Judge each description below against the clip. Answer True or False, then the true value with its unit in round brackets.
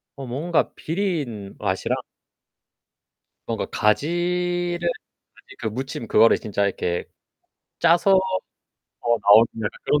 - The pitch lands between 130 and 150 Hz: True (135 Hz)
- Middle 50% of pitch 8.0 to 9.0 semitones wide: True (8.3 semitones)